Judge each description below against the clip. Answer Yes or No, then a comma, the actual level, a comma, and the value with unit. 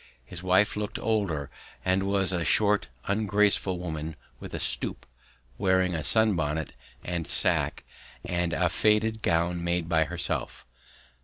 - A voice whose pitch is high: No, very low, 90 Hz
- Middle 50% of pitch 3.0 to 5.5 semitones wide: Yes, average, 3.3 semitones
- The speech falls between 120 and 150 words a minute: Yes, average, 140 wpm